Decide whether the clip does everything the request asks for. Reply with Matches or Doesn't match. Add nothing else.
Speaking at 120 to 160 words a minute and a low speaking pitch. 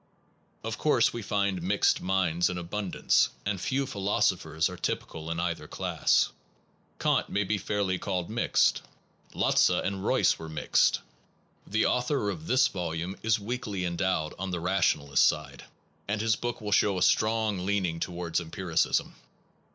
Matches